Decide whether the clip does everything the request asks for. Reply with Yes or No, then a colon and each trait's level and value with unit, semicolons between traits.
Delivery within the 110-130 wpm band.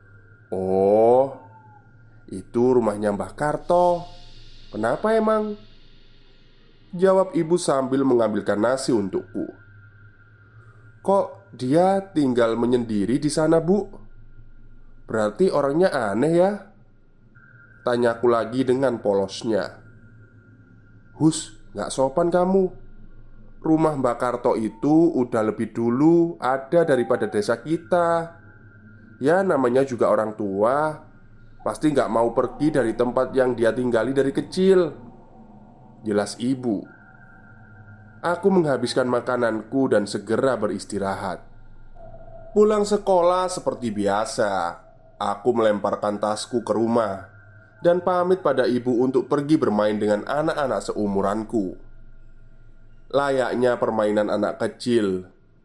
No: average, 95 wpm